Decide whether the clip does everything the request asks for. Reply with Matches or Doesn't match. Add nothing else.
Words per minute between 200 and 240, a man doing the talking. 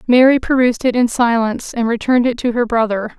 Doesn't match